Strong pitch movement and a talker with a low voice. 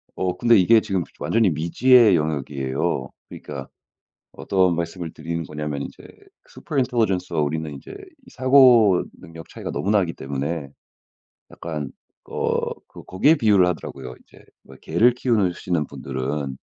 Yes: wide, 6.1 semitones; very low, 85 Hz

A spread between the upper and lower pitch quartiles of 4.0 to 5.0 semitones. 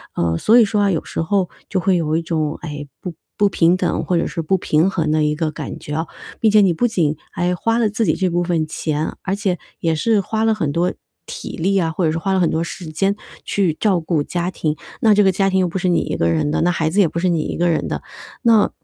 No: average, 3.6 semitones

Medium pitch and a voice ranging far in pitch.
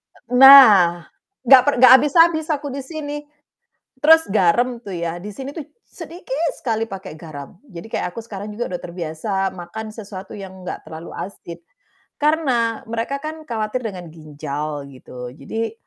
No: high, 215 Hz; wide, 7.5 semitones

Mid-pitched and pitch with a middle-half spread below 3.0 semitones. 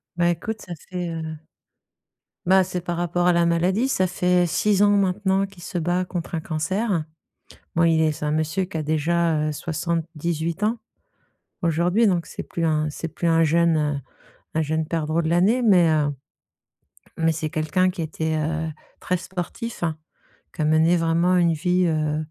Yes: medium, 170 Hz; narrow, 2.4 semitones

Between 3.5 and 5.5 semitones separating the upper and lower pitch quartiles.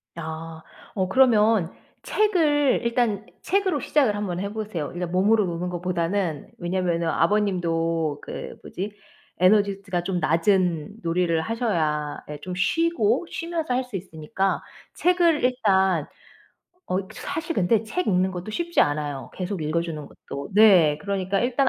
Yes: average, 5.1 semitones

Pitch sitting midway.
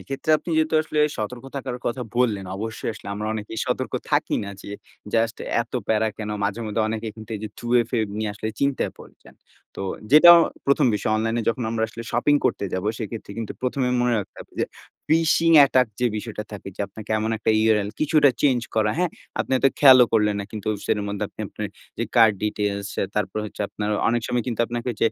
No: low, 115 Hz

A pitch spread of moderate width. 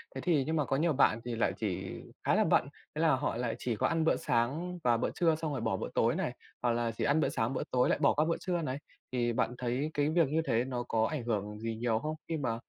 Yes: average, 5.0 semitones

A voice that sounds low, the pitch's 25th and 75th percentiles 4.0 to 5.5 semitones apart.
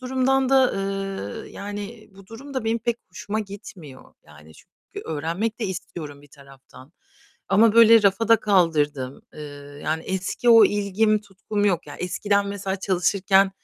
No: high, 195 Hz; average, 5.2 semitones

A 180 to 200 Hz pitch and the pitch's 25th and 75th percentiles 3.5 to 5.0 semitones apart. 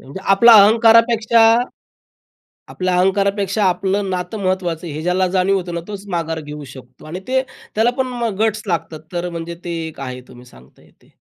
Yes: medium, 185 Hz; average, 4.2 semitones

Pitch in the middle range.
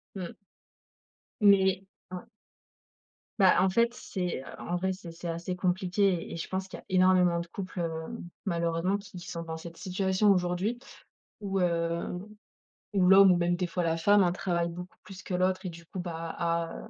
Yes: medium, 180 Hz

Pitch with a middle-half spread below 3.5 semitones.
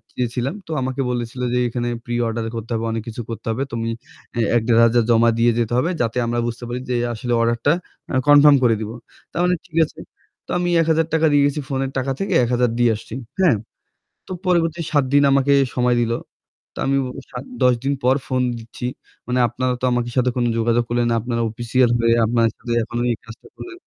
Yes: average, 2.8 semitones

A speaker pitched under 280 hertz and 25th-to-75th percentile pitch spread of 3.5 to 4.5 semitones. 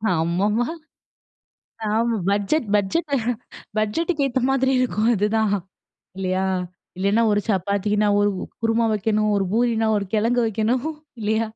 No: high, 215 Hz; narrow, 2.5 semitones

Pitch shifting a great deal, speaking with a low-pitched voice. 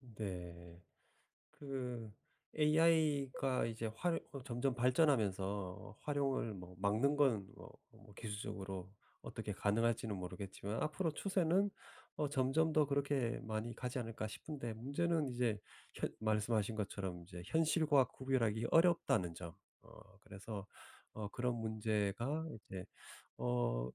Yes: wide, 5.7 semitones; low, 115 Hz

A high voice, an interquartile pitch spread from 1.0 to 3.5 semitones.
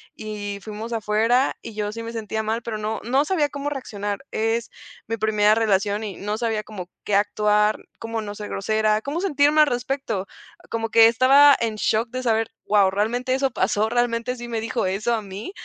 Yes: high, 225 Hz; narrow, 2.5 semitones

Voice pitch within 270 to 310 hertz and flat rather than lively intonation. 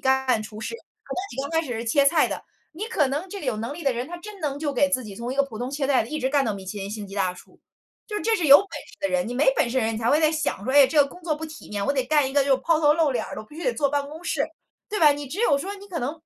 No: very high, 280 Hz; average, 4.0 semitones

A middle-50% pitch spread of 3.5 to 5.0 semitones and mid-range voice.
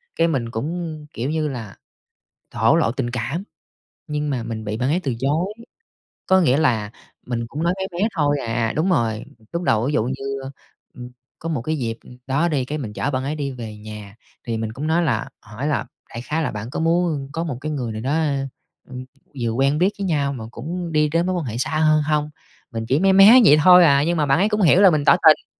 No: wide, 5.4 semitones; medium, 145 Hz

